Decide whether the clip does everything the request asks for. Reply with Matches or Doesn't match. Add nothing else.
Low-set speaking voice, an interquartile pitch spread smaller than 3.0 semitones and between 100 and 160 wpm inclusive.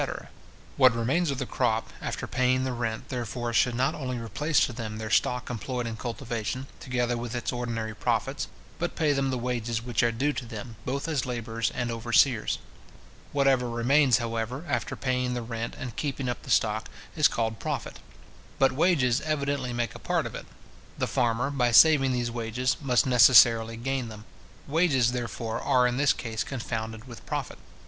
Doesn't match